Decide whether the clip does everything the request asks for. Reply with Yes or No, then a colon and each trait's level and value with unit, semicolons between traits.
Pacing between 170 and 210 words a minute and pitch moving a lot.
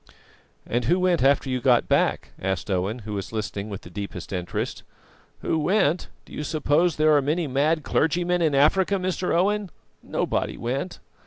Yes: average, 180 wpm; wide, 7.0 semitones